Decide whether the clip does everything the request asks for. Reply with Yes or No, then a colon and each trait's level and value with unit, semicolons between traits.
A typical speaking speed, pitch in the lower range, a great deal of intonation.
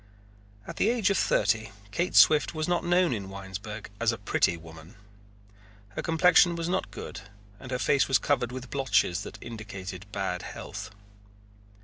Yes: average, 160 wpm; low, 115 Hz; wide, 8.9 semitones